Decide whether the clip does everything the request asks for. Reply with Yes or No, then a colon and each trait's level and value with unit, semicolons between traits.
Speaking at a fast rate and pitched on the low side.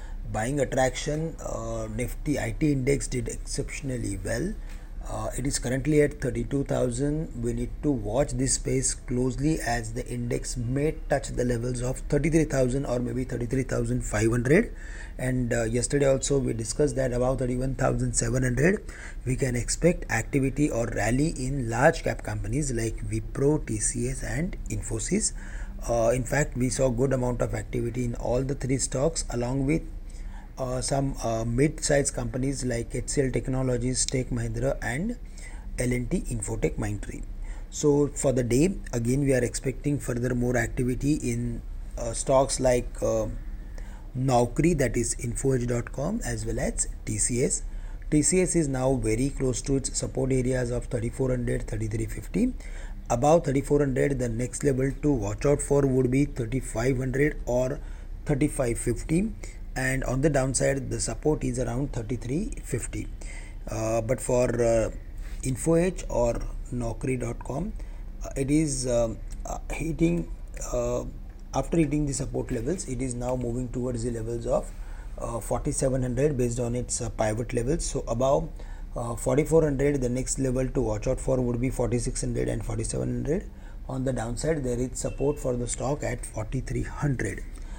No: average, 140 wpm; low, 125 Hz